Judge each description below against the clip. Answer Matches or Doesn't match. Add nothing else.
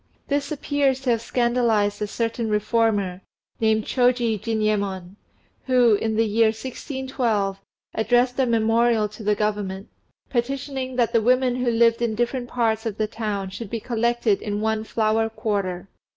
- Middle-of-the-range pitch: Doesn't match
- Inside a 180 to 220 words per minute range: Doesn't match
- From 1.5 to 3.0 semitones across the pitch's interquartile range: Matches